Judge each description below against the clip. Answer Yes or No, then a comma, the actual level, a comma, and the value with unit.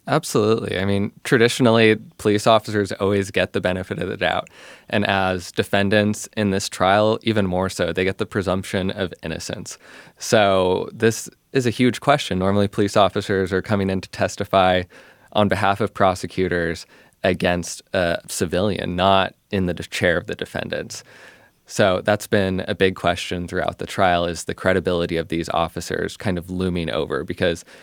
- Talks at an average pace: Yes, average, 165 wpm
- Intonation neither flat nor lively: No, narrow, 2.3 semitones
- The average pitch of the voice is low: Yes, very low, 95 Hz